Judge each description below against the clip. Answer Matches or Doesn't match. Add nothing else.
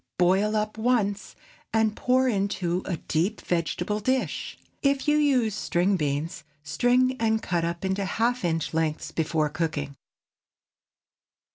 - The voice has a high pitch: Matches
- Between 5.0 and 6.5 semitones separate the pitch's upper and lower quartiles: Matches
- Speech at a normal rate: Doesn't match